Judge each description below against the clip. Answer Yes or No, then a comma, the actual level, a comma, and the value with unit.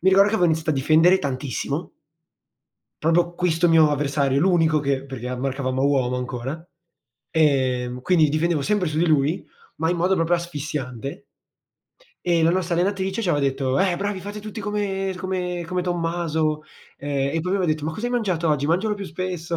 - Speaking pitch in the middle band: Yes, medium, 165 Hz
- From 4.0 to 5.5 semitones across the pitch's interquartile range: Yes, average, 4.3 semitones